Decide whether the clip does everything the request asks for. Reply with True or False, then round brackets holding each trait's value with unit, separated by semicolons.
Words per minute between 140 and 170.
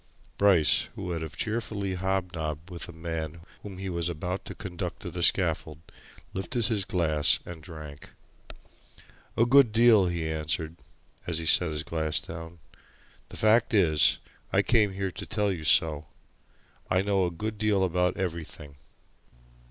True (155 wpm)